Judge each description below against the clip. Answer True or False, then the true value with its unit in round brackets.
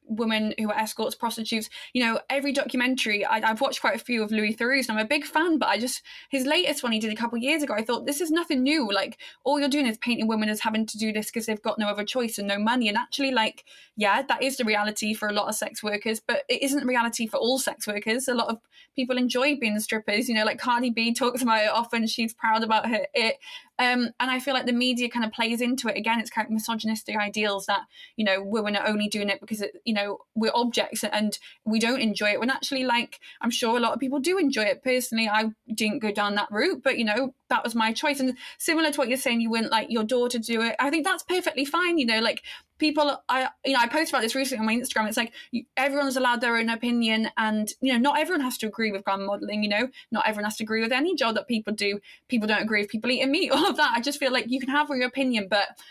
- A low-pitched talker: False (235 Hz)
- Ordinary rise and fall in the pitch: True (3.4 semitones)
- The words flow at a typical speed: False (270 wpm)